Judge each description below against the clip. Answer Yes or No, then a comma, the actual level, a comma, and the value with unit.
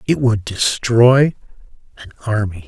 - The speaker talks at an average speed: No, slow, 110 wpm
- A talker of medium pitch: No, low, 115 Hz